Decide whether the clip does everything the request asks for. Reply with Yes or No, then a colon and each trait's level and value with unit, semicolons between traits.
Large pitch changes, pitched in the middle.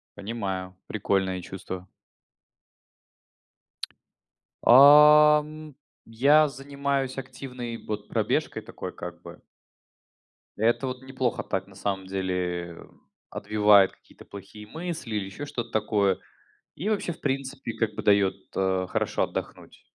No: wide, 6.1 semitones; low, 115 Hz